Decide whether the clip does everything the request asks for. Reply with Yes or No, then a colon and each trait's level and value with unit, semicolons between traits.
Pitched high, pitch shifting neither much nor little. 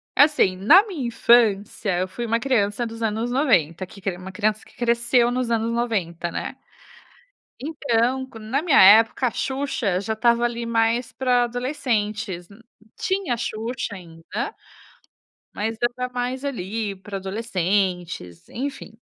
Yes: high, 230 Hz; average, 3.7 semitones